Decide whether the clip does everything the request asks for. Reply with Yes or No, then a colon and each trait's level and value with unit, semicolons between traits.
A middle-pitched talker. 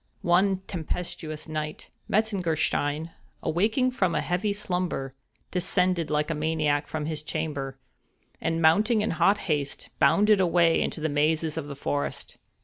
Yes: medium, 165 Hz